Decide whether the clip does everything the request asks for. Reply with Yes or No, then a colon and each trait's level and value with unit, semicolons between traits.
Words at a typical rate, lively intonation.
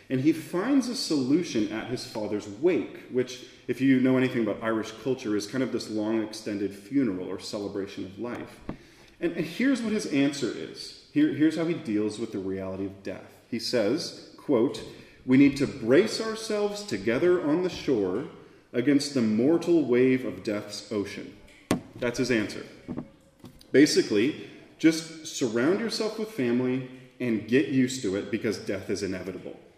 Yes: average, 165 wpm; wide, 8.4 semitones